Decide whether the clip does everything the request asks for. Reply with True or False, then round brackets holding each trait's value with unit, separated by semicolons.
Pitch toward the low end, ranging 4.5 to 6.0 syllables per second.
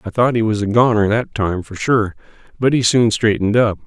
True (110 Hz; 5.5 syllables/s)